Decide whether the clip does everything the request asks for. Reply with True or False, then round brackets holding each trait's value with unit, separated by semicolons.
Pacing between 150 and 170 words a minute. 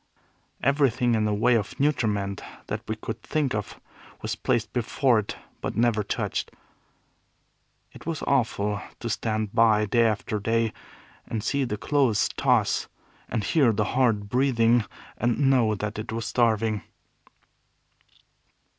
False (140 wpm)